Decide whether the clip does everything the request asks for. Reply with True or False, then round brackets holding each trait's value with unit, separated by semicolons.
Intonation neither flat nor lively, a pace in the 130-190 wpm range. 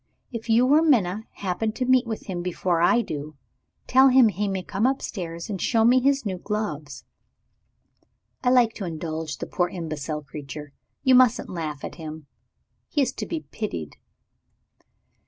False (7.4 semitones; 165 wpm)